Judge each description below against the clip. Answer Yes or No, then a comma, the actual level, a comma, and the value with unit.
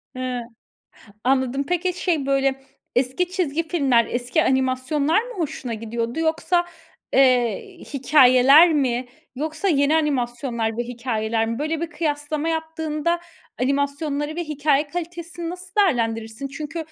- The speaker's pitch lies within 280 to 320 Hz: Yes, very high, 285 Hz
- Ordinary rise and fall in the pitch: Yes, average, 4.3 semitones